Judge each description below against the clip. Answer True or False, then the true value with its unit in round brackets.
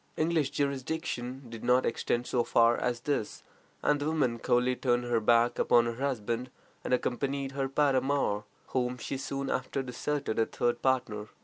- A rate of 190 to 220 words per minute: False (170 wpm)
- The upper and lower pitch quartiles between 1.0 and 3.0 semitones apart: True (2.5 semitones)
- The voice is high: False (125 Hz)